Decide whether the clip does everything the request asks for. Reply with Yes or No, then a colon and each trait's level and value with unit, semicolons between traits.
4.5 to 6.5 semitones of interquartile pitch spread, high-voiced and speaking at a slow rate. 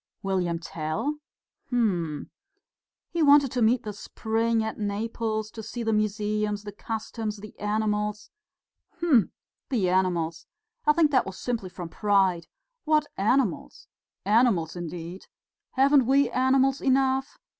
Yes: average, 4.9 semitones; high, 215 Hz; slow, 125 wpm